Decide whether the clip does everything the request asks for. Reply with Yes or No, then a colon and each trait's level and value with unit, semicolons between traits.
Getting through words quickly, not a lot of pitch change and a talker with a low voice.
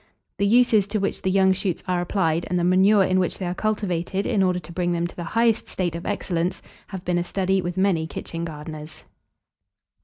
No: fast, 215 wpm; narrow, 2.3 semitones; medium, 185 Hz